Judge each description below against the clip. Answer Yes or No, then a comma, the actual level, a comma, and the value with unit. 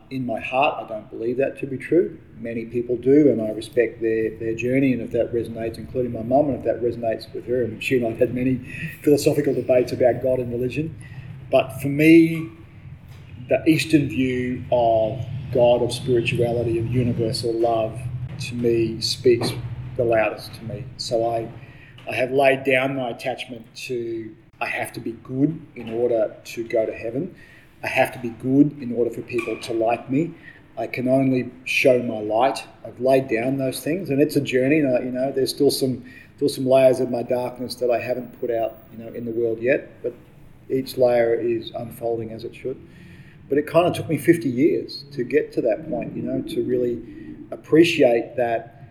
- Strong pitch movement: No, narrow, 2.5 semitones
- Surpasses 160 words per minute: Yes, average, 200 wpm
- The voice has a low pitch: Yes, low, 125 Hz